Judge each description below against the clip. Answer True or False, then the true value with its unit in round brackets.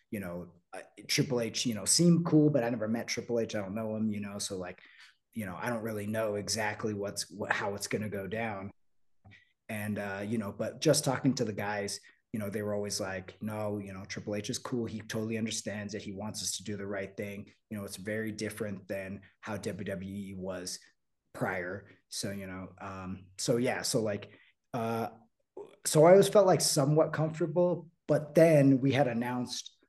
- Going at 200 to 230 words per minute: True (205 wpm)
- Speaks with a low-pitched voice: True (110 Hz)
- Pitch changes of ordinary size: True (3.6 semitones)